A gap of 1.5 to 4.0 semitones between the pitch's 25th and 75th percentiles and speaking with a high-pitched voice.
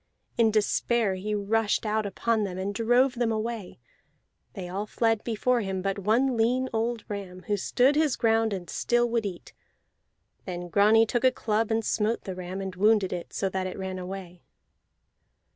Yes: average, 3.2 semitones; high, 215 Hz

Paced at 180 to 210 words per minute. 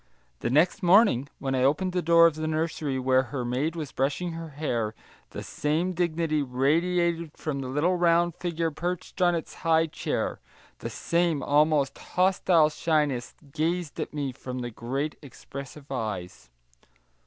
No: average, 155 wpm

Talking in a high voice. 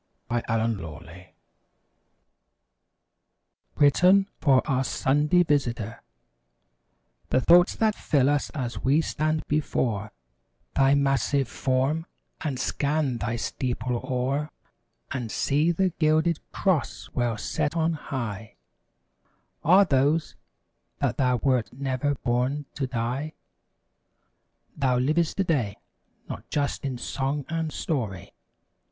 No: low, 135 Hz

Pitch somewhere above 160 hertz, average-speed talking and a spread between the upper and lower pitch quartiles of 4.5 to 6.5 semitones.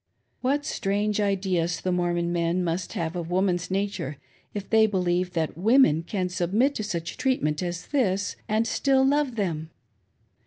No: medium, 185 Hz; average, 160 wpm; average, 3.8 semitones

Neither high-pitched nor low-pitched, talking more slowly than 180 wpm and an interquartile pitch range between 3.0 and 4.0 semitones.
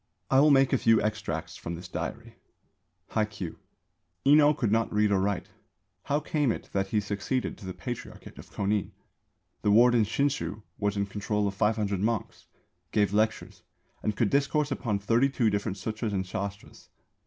No: low, 105 Hz; average, 170 wpm; average, 3.3 semitones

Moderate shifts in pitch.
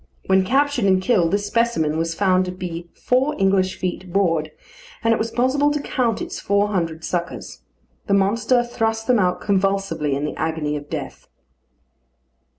Yes: average, 5.0 semitones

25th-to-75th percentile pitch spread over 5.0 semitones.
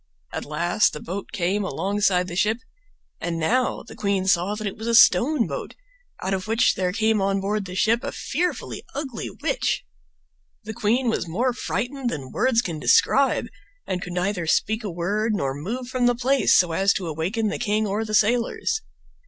No: average, 4.3 semitones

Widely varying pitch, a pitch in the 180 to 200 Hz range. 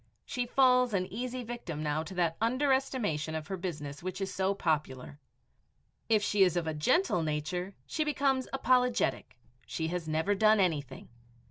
Yes: wide, 7.7 semitones; high, 190 Hz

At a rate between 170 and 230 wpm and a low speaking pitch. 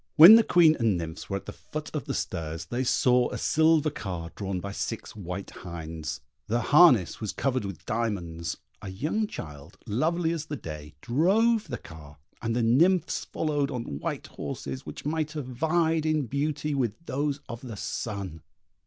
Yes: average, 180 wpm; low, 120 Hz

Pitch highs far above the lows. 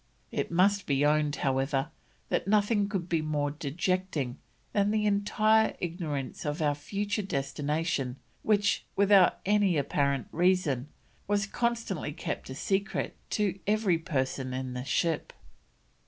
Yes: wide, 5.8 semitones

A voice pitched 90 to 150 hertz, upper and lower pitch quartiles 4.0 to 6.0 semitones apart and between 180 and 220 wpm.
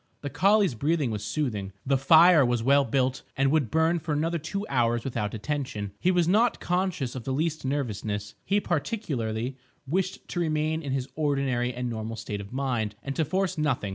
Yes: medium, 140 Hz; average, 5.2 semitones; average, 190 wpm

